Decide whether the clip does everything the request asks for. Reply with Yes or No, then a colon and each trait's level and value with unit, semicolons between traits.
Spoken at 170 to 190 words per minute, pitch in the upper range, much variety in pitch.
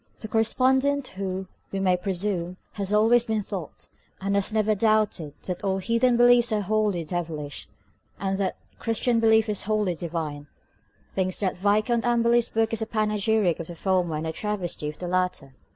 No: average, 175 wpm; high, 200 Hz; average, 3.6 semitones